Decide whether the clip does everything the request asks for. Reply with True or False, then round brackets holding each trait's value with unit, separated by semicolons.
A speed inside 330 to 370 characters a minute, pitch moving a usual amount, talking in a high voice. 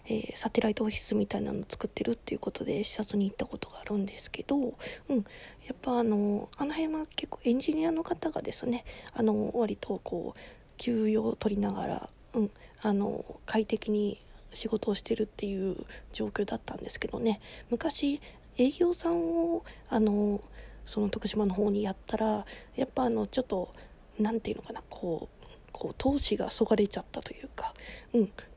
True (345 characters per minute; 3.4 semitones; 225 Hz)